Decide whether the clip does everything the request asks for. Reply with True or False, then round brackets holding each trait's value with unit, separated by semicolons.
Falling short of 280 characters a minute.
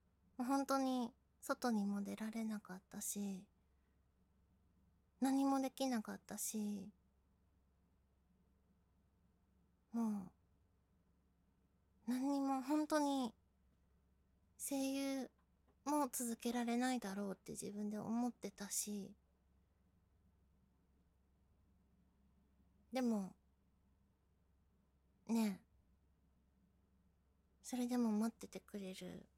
True (140 characters per minute)